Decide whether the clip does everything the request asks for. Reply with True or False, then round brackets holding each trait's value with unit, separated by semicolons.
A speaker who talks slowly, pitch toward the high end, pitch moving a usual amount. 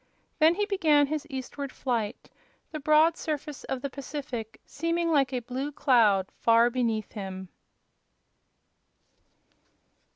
True (120 wpm; 275 Hz; 4.7 semitones)